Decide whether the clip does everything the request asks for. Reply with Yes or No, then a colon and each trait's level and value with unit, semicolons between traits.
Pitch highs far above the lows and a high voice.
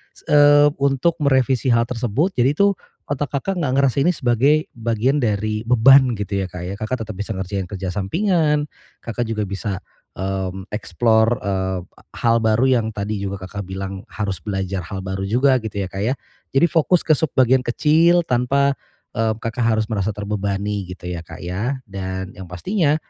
No: wide, 5.7 semitones; low, 110 Hz